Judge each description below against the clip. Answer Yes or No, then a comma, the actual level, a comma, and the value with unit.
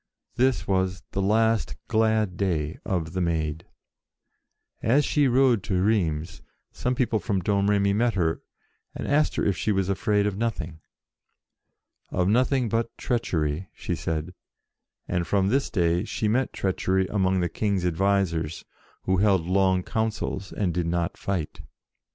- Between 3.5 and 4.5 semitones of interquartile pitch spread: Yes, average, 3.9 semitones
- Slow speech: No, average, 150 wpm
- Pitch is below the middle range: Yes, very low, 95 Hz